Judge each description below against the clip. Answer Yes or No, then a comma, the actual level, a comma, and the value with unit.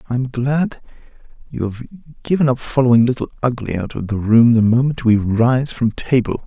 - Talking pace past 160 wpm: Yes, average, 185 wpm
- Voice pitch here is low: Yes, low, 125 Hz